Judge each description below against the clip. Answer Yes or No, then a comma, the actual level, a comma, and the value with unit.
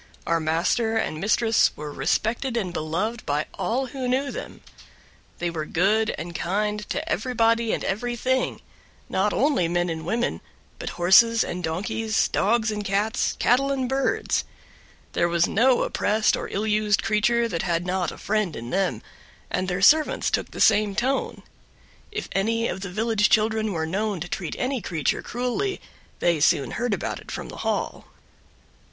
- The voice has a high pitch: Yes, high, 210 Hz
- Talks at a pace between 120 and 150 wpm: No, average, 165 wpm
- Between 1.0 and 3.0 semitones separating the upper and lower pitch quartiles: No, average, 5.1 semitones